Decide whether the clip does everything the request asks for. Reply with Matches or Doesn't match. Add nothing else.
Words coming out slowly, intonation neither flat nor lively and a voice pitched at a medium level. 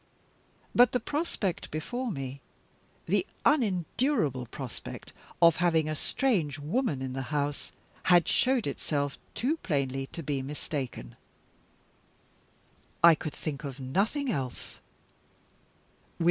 Doesn't match